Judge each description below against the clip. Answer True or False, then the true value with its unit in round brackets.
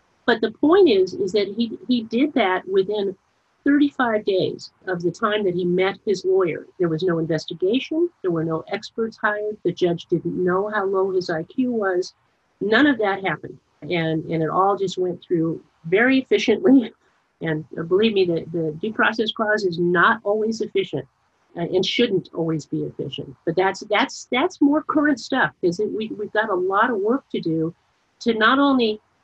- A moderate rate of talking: True (180 wpm)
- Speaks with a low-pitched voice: False (200 Hz)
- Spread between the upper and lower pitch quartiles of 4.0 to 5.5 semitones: True (4.8 semitones)